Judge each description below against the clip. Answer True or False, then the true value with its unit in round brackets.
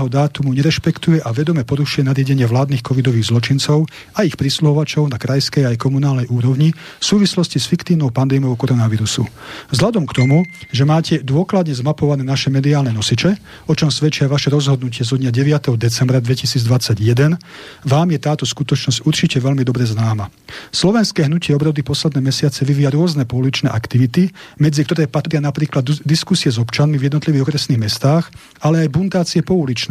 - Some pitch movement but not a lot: True (3.1 semitones)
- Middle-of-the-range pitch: True (145 Hz)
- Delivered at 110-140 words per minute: False (155 wpm)